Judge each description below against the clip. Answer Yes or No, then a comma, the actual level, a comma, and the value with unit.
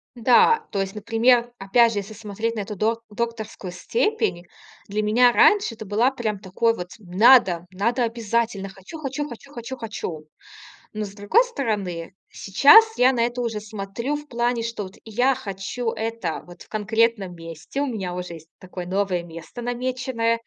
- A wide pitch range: No, average, 3.8 semitones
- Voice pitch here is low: No, high, 225 Hz